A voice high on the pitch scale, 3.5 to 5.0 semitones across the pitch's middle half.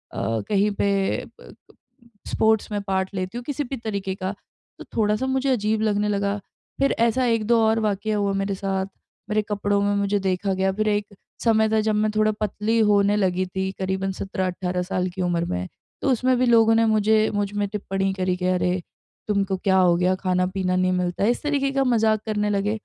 No: high, 205 Hz; narrow, 2.5 semitones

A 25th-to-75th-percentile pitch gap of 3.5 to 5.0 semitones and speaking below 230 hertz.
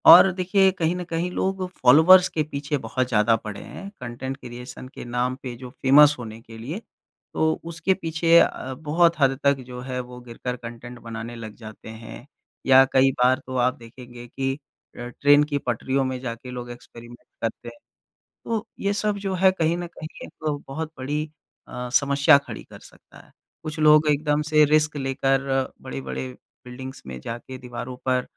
Yes: average, 4.2 semitones; low, 135 Hz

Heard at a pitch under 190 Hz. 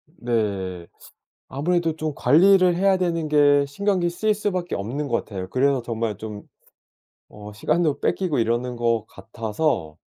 Yes: medium, 140 Hz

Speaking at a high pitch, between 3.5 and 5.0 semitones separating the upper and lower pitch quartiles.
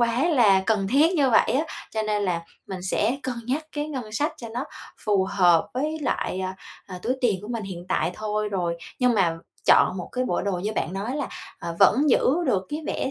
No: high, 215 Hz; wide, 5.4 semitones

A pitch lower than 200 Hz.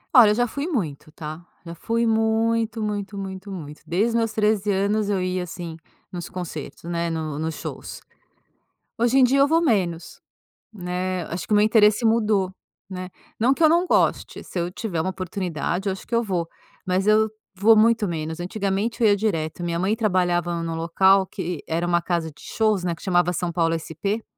Yes: high, 190 Hz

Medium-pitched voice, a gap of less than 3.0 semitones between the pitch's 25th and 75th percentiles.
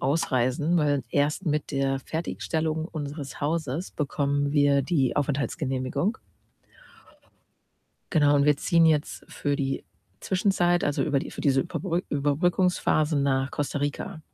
Yes: medium, 145 Hz; narrow, 2.6 semitones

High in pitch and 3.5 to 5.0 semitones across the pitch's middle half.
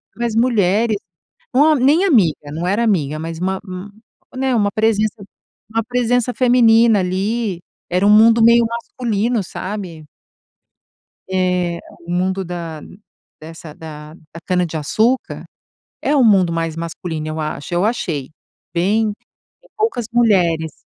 No: high, 200 Hz; wide, 5.5 semitones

